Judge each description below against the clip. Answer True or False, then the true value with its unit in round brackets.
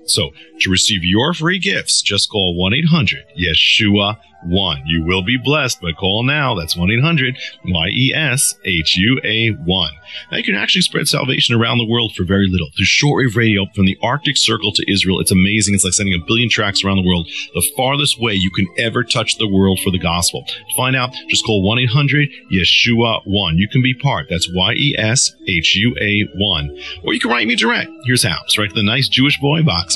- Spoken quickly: True (225 wpm)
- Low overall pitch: True (105 Hz)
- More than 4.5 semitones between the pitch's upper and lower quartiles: True (5.5 semitones)